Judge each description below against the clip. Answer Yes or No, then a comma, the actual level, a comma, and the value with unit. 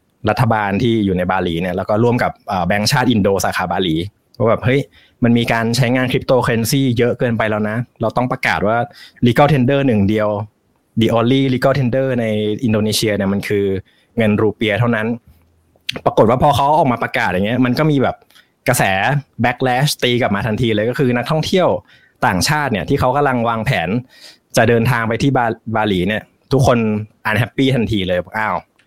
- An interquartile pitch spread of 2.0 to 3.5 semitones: Yes, average, 3.2 semitones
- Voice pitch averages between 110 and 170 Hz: Yes, low, 115 Hz